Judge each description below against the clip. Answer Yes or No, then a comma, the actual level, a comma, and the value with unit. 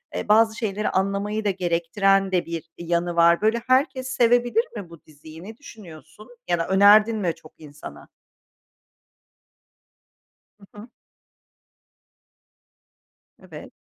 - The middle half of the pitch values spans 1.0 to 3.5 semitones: No, average, 4.4 semitones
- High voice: Yes, high, 195 Hz